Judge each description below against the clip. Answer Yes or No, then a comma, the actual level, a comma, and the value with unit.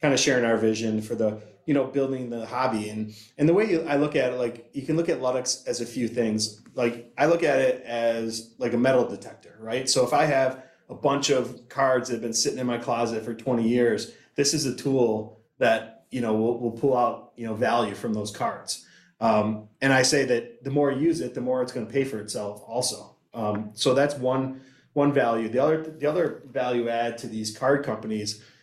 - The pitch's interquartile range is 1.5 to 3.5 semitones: Yes, average, 2.8 semitones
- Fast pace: Yes, fast, 235 wpm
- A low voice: Yes, low, 120 Hz